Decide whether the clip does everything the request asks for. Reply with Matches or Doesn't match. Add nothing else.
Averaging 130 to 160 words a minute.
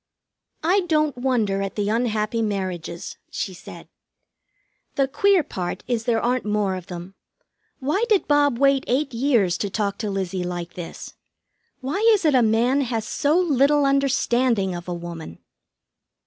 Matches